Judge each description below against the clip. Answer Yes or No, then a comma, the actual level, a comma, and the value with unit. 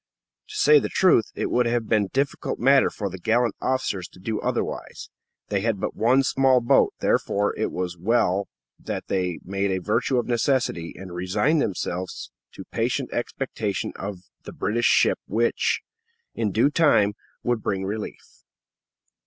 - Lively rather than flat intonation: No, average, 4.2 semitones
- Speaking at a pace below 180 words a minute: Yes, average, 160 wpm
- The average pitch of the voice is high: No, low, 110 Hz